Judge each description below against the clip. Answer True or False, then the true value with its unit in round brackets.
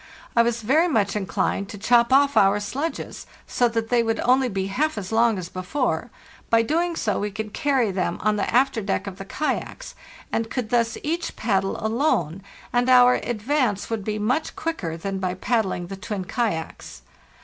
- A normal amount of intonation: True (4.3 semitones)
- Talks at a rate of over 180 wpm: True (190 wpm)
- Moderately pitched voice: False (225 Hz)